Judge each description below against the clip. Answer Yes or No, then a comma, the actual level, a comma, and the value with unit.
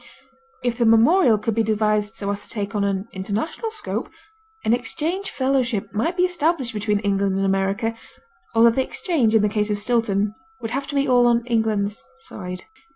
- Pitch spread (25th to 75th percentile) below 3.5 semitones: No, average, 3.8 semitones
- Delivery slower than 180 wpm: No, average, 185 wpm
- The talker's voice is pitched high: Yes, high, 225 Hz